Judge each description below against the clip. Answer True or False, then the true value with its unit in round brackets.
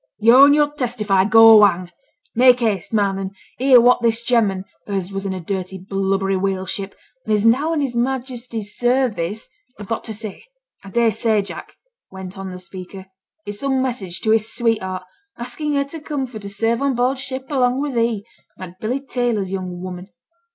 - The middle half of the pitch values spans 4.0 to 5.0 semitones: True (4.4 semitones)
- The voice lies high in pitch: True (220 Hz)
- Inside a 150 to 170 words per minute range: False (190 wpm)